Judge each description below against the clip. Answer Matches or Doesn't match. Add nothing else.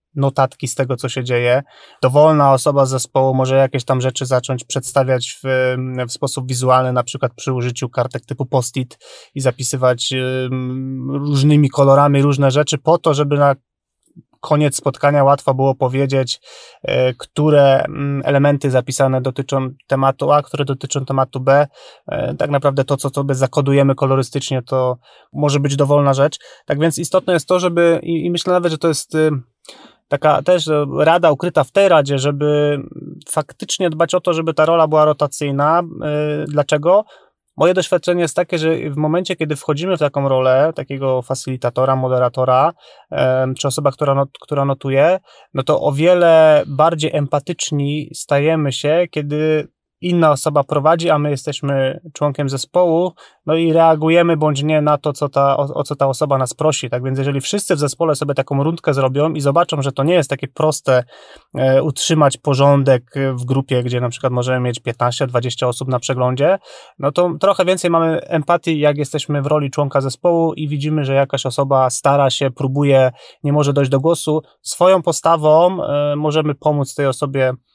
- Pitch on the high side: Doesn't match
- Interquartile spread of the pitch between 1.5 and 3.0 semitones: Matches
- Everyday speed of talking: Doesn't match